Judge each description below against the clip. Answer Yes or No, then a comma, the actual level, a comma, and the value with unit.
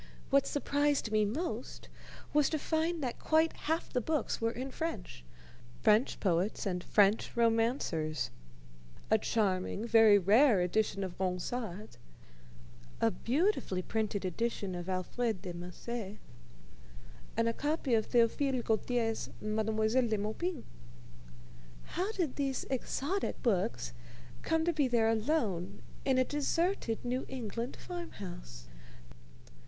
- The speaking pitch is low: No, high, 230 Hz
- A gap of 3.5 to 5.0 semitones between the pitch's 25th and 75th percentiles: No, wide, 5.4 semitones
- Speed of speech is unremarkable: No, slow, 125 wpm